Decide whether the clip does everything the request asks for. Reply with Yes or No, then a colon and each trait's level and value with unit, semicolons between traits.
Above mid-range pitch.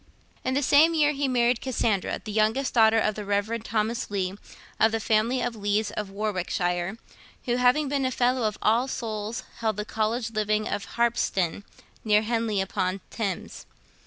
Yes: high, 220 Hz